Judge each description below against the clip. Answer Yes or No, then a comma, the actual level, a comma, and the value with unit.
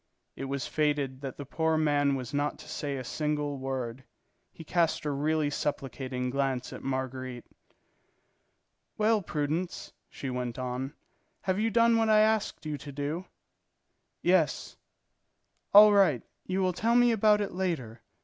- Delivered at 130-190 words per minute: Yes, average, 150 wpm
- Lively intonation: Yes, wide, 5.7 semitones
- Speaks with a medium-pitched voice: Yes, medium, 150 Hz